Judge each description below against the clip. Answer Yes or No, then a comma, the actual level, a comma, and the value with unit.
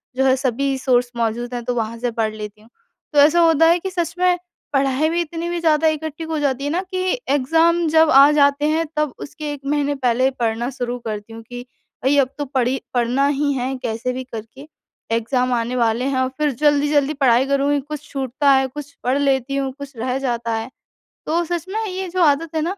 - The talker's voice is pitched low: No, very high, 275 Hz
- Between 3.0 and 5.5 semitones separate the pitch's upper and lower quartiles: Yes, average, 3.6 semitones